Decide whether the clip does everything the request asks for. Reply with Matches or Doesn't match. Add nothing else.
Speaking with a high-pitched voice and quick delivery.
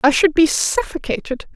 Doesn't match